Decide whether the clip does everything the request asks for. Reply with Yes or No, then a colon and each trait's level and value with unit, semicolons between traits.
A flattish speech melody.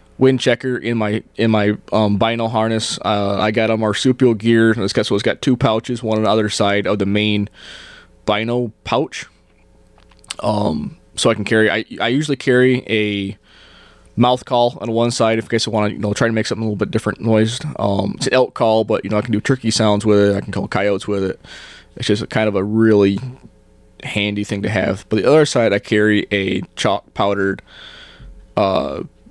Yes: narrow, 2.2 semitones